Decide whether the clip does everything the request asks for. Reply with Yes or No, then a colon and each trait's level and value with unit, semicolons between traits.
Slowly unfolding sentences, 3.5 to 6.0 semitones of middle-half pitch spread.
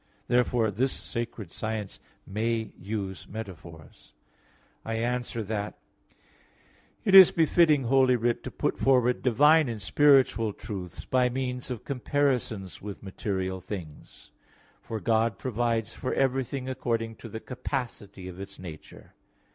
Yes: slow, 125 wpm; average, 4.0 semitones